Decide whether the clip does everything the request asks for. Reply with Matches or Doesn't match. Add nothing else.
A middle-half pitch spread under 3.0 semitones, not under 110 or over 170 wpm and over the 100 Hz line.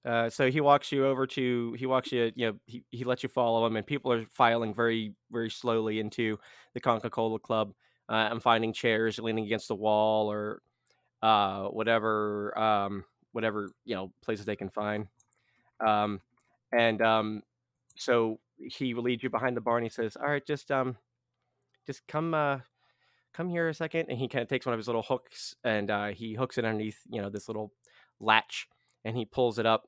Doesn't match